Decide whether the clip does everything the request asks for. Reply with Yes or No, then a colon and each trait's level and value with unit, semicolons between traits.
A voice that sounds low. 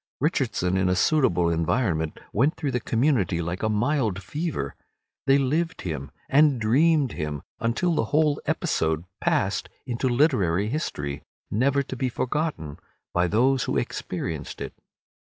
Yes: low, 115 Hz